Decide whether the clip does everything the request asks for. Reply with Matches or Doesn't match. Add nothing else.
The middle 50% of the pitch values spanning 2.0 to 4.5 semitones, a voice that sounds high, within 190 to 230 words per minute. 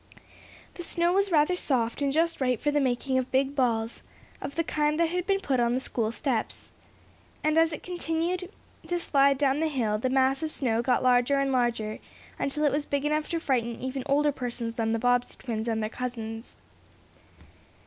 Matches